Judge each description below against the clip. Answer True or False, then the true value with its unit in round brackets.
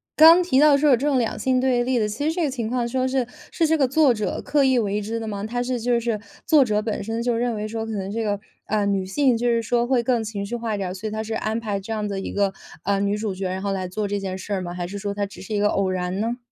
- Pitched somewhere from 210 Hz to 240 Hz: True (220 Hz)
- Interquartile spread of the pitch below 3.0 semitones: False (3.5 semitones)